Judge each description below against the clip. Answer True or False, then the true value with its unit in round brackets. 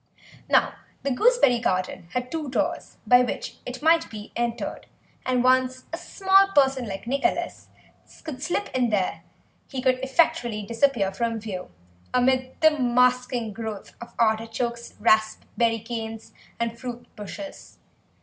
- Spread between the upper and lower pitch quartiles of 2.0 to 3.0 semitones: True (2.7 semitones)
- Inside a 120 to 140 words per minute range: True (135 wpm)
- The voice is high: True (245 Hz)